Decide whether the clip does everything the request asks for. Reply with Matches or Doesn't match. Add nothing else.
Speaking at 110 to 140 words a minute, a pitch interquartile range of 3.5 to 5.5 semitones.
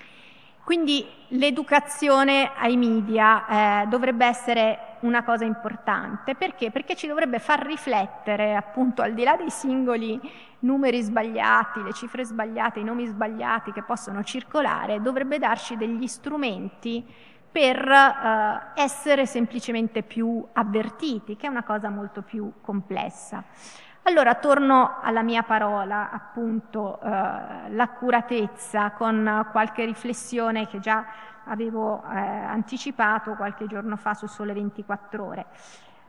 Doesn't match